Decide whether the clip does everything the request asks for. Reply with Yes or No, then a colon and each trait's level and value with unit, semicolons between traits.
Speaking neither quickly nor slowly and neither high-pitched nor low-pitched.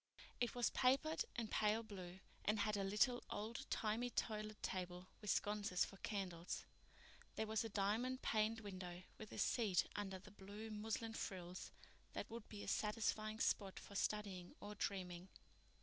No: average, 160 wpm; high, 210 Hz